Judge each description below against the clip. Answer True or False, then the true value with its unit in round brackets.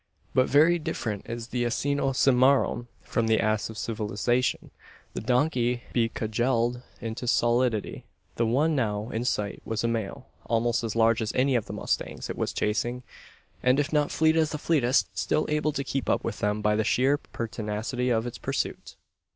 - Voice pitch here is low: True (120 Hz)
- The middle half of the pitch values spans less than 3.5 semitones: True (3.0 semitones)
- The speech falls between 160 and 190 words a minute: True (180 wpm)